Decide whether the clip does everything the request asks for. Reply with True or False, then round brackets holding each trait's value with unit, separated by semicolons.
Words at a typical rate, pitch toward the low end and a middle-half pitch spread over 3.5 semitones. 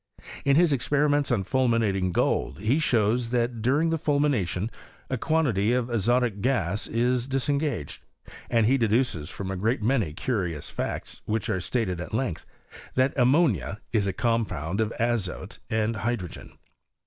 True (150 wpm; 115 Hz; 4.7 semitones)